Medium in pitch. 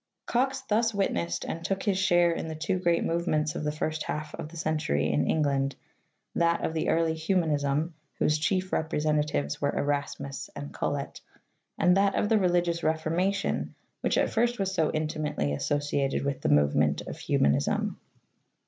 Yes: medium, 155 Hz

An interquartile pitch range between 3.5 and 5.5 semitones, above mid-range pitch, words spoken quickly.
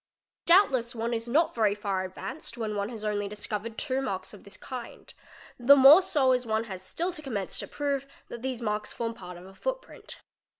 Yes: average, 4.5 semitones; high, 230 Hz; fast, 210 wpm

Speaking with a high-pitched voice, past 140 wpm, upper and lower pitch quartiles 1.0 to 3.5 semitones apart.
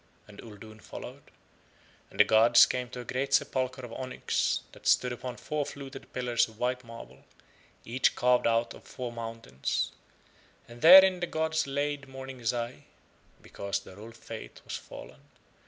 No: low, 125 Hz; average, 155 wpm; narrow, 2.5 semitones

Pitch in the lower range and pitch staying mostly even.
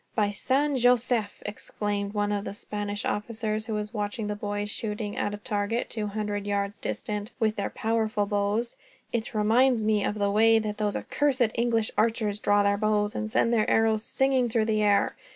No: high, 215 Hz; narrow, 1.7 semitones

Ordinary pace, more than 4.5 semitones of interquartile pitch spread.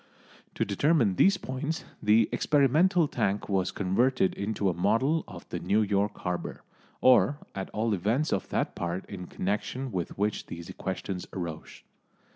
Yes: average, 150 wpm; wide, 5.6 semitones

